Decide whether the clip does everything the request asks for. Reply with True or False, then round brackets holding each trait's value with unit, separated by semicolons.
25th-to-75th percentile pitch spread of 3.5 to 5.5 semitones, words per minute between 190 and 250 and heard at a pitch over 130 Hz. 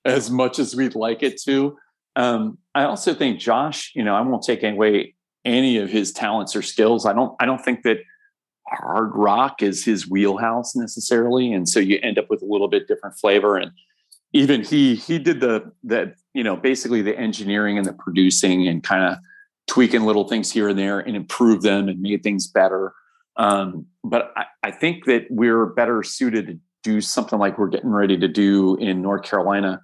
False (4.7 semitones; 200 wpm; 115 Hz)